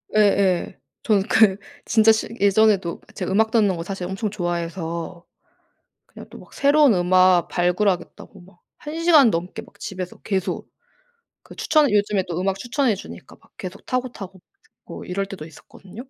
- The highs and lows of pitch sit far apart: No, average, 3.4 semitones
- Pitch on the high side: Yes, high, 195 Hz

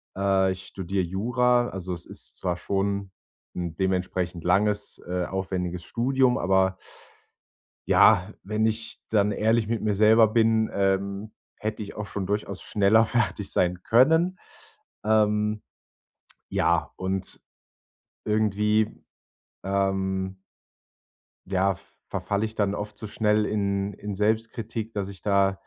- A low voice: Yes, low, 100 Hz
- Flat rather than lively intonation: Yes, narrow, 2.3 semitones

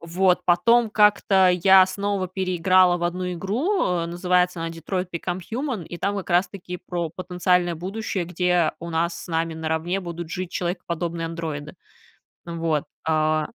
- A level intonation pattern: Yes, narrow, 2.0 semitones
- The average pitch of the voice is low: No, medium, 180 Hz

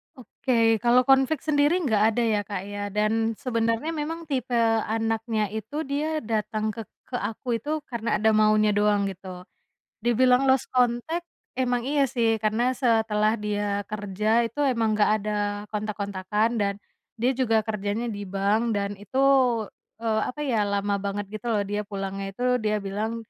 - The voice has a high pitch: Yes, high, 220 Hz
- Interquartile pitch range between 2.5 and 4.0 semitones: Yes, average, 3.1 semitones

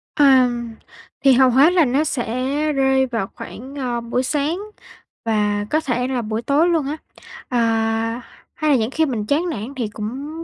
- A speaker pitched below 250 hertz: No, very high, 265 Hz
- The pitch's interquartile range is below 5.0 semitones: Yes, average, 3.9 semitones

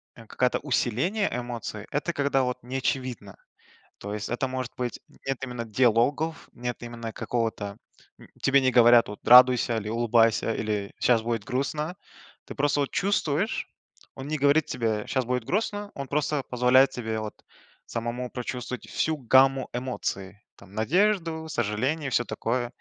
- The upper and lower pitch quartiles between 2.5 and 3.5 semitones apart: Yes, average, 3.2 semitones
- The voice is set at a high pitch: No, low, 125 Hz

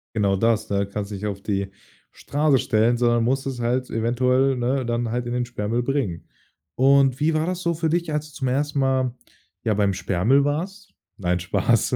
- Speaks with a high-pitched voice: No, low, 125 Hz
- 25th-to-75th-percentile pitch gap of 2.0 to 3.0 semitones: No, average, 4.4 semitones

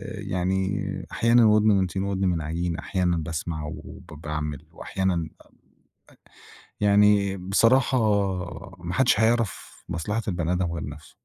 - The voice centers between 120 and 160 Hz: No, very low, 95 Hz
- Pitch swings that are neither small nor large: Yes, average, 3.6 semitones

